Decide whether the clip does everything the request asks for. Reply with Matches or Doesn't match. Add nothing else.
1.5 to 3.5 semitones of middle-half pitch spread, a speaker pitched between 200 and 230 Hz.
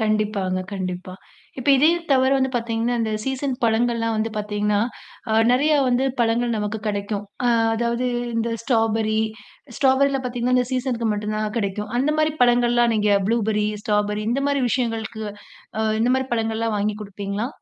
Matches